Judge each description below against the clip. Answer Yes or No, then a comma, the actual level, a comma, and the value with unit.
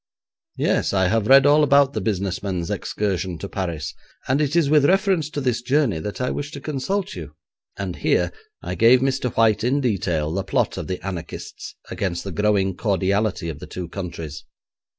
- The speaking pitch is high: No, low, 105 Hz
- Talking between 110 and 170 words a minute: No, average, 190 wpm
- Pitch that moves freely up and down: Yes, wide, 6.8 semitones